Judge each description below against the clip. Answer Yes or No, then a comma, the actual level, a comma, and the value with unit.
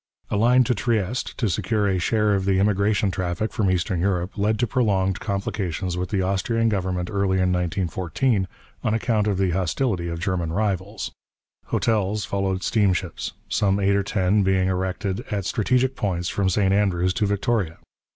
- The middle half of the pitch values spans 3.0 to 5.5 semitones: No, narrow, 2.4 semitones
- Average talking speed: Yes, average, 170 wpm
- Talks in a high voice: No, low, 100 Hz